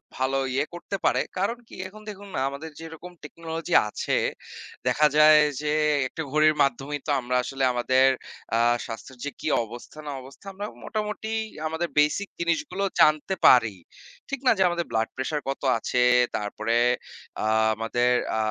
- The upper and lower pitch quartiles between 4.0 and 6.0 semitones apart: Yes, average, 4.9 semitones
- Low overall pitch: No, medium, 150 Hz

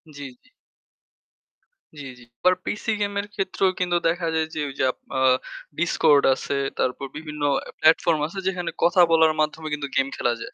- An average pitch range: Yes, average, 3.6 semitones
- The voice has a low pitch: No, medium, 160 Hz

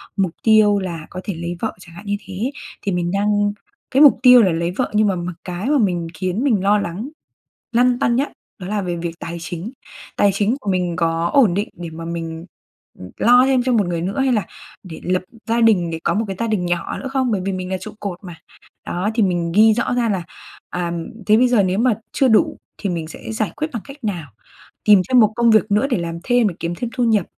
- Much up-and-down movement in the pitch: No, average, 4.7 semitones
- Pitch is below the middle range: No, high, 200 Hz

